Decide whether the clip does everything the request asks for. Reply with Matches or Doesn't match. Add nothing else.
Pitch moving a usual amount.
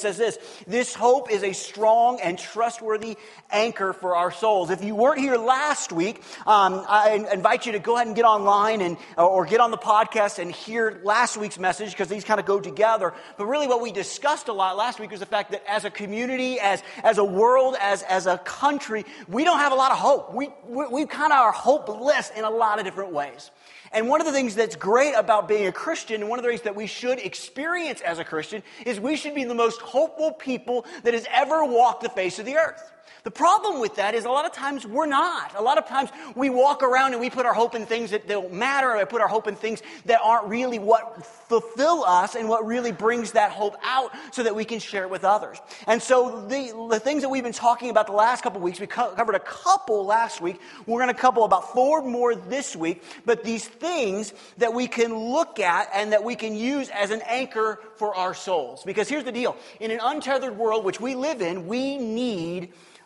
Matches